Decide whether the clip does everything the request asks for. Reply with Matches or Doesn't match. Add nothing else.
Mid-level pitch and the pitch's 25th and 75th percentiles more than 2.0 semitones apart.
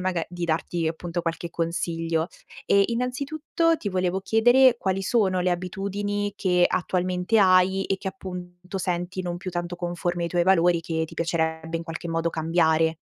Matches